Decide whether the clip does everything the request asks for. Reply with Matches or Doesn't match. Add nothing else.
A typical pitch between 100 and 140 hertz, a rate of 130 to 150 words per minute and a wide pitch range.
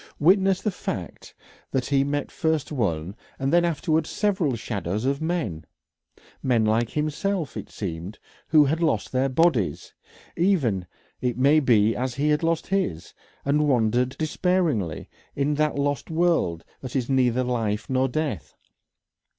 Matches